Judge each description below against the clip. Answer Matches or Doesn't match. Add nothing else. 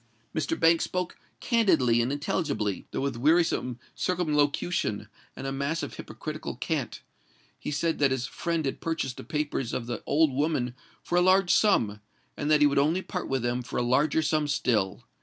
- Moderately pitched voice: Matches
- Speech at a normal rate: Matches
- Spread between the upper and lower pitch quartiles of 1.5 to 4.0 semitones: Doesn't match